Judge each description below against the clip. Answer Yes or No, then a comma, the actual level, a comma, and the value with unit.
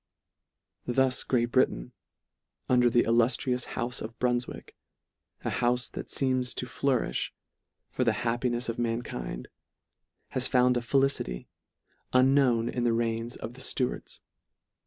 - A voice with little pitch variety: Yes, narrow, 1.5 semitones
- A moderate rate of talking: No, slow, 125 wpm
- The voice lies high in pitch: No, low, 120 Hz